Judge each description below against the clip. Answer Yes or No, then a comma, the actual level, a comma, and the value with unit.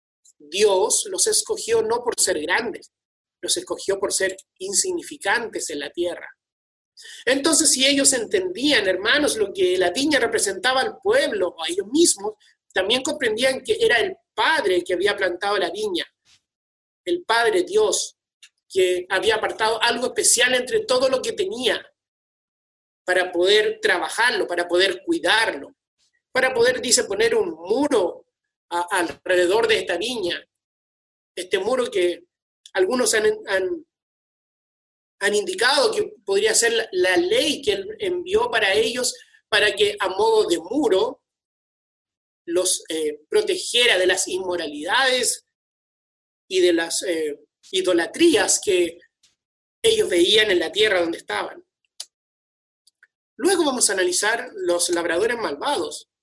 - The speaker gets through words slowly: Yes, slow, 130 wpm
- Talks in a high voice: Yes, very high, 360 Hz